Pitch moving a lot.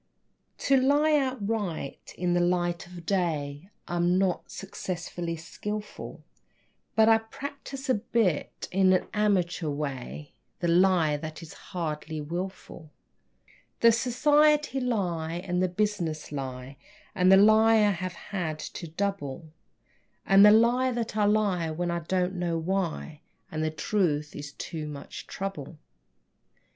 No: average, 4.7 semitones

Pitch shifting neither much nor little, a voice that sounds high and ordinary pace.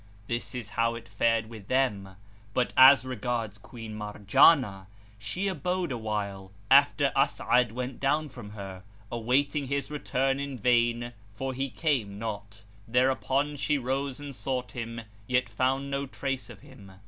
No: average, 4.0 semitones; low, 125 Hz; average, 150 wpm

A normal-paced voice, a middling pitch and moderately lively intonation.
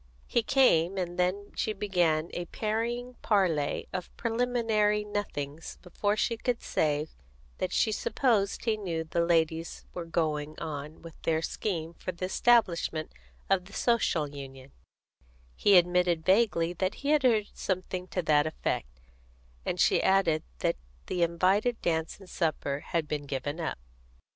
Yes: average, 150 wpm; medium, 180 Hz; average, 4.6 semitones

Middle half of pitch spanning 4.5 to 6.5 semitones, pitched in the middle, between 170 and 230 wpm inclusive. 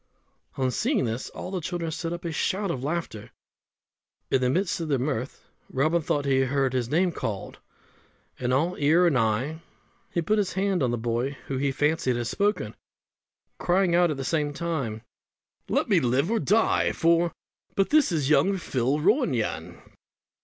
Yes: average, 5.1 semitones; medium, 150 Hz; average, 180 wpm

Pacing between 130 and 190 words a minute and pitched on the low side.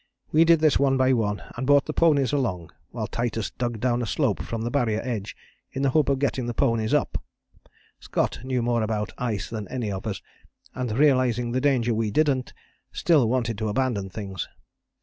No: average, 200 wpm; low, 120 Hz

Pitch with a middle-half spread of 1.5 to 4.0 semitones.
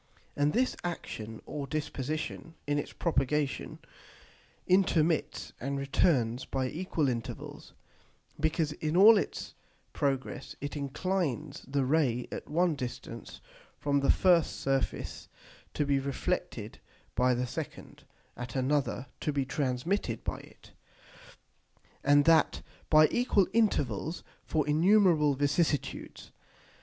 Yes: average, 3.4 semitones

